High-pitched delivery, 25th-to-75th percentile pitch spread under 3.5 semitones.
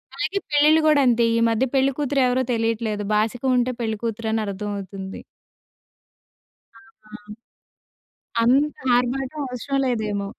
No: high, 235 Hz; average, 4.1 semitones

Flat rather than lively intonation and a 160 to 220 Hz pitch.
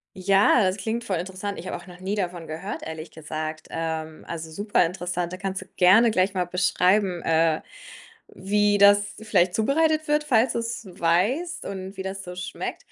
No: average, 3.0 semitones; high, 190 Hz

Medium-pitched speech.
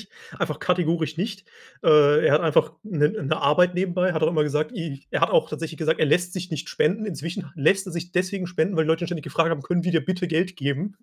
Yes: medium, 165 Hz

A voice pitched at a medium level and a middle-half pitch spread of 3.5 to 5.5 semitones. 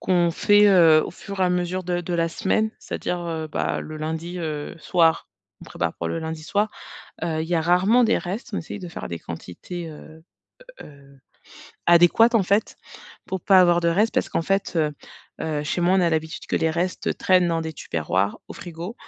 No: medium, 170 Hz; average, 2.7 semitones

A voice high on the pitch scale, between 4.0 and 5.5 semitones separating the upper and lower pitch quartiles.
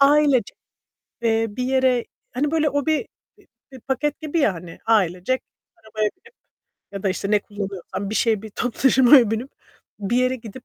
Yes: high, 240 Hz; average, 4.6 semitones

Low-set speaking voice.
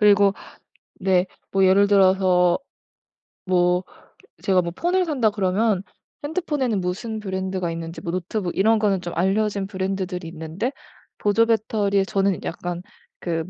No: high, 195 Hz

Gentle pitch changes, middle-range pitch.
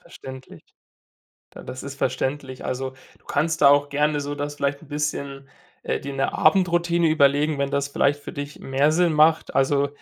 Yes: narrow, 1.5 semitones; medium, 145 Hz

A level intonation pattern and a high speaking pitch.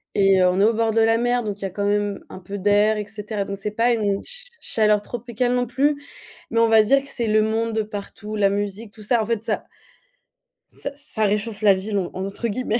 Yes: narrow, 2.1 semitones; high, 215 Hz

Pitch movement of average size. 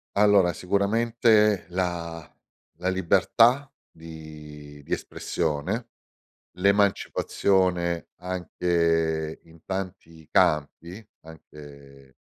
Yes: average, 3.8 semitones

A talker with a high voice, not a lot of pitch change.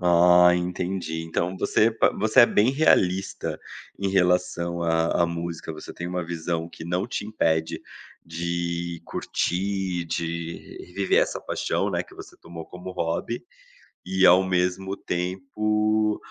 No: very low, 90 Hz; narrow, 2.2 semitones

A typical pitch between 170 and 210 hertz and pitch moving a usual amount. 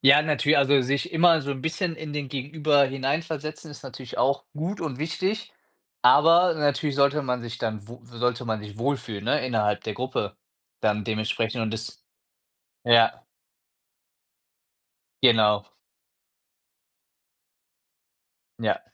No: low, 135 Hz; average, 4.6 semitones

